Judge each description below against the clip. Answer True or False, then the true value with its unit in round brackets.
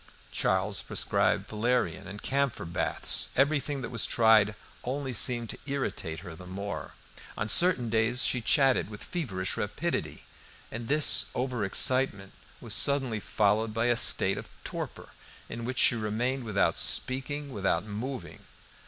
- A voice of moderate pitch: False (115 Hz)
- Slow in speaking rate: False (145 wpm)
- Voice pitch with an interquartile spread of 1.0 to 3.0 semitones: False (4.2 semitones)